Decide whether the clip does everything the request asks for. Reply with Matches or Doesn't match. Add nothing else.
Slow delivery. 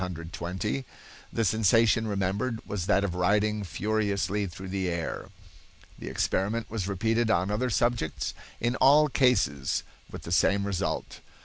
Matches